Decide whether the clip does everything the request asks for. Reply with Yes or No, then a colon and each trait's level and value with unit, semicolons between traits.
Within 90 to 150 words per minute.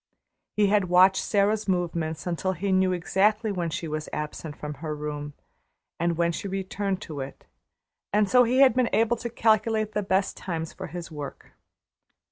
No: average, 175 wpm